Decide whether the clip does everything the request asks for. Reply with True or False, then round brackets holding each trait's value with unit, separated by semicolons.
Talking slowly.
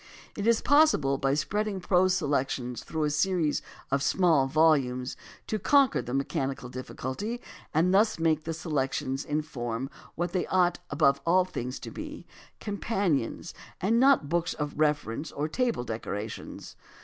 False (150 wpm)